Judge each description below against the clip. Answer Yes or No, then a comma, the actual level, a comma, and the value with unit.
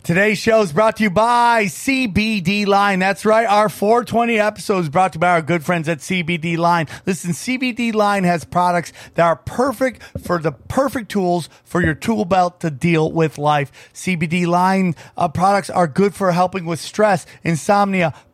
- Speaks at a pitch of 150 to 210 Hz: Yes, medium, 185 Hz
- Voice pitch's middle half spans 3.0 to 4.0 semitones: Yes, average, 3.7 semitones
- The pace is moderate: Yes, average, 180 wpm